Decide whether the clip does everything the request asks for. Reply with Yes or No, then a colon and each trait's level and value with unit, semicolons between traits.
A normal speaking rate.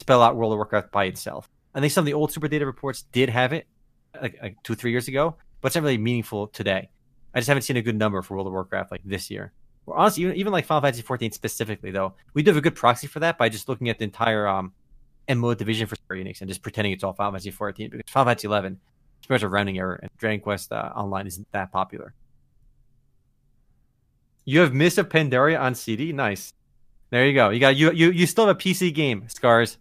No: fast, 245 wpm